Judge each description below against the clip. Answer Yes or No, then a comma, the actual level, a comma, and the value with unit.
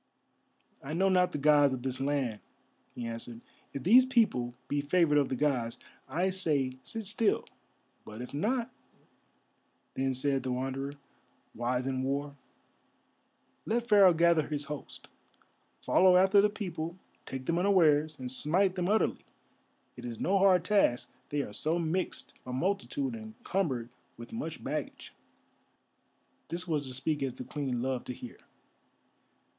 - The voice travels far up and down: Yes, wide, 6.1 semitones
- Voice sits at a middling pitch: Yes, medium, 150 Hz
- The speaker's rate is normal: Yes, average, 150 wpm